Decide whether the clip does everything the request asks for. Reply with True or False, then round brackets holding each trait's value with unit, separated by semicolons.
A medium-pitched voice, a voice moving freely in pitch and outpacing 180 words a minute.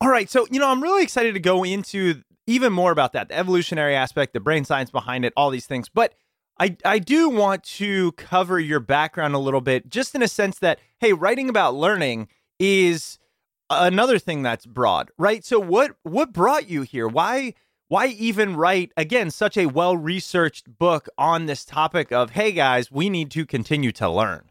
True (175 Hz; 6.5 semitones; 195 wpm)